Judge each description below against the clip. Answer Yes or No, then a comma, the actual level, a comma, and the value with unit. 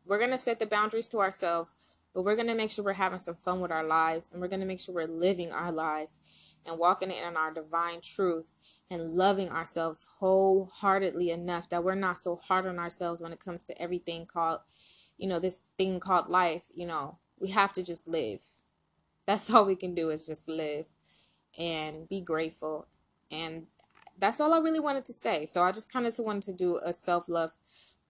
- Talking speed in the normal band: No, fast, 210 wpm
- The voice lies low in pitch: No, medium, 175 Hz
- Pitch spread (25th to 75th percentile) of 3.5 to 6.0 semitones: No, average, 2.7 semitones